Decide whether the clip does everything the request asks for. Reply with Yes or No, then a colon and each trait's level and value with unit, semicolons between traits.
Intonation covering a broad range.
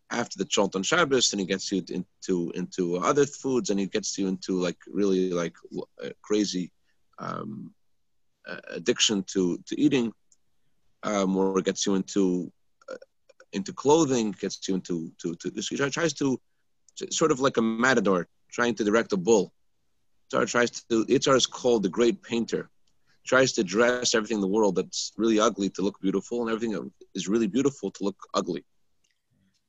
No: average, 4.0 semitones